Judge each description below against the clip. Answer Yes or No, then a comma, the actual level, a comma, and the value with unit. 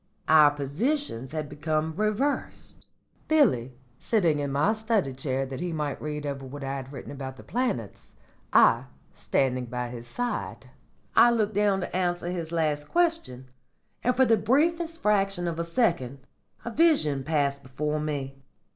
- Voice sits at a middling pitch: Yes, medium, 155 Hz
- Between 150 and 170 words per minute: Yes, average, 155 wpm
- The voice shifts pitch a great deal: Yes, wide, 7.8 semitones